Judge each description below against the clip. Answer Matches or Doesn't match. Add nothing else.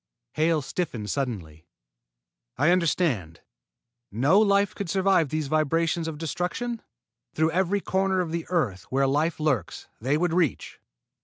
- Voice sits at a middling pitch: Matches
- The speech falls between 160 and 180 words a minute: Doesn't match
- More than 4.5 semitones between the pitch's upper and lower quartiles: Matches